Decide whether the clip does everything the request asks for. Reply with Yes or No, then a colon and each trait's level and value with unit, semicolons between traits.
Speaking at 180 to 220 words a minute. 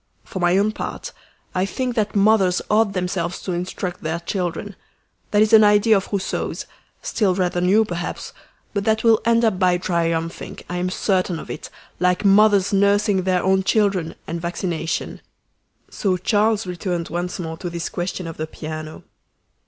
No: average, 165 wpm